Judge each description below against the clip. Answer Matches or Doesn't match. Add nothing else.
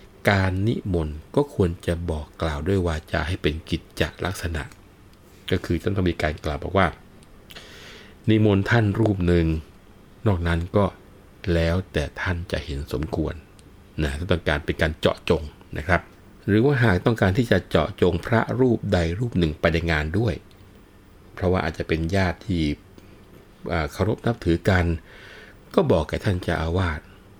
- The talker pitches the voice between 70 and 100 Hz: Matches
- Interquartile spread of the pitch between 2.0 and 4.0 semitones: Matches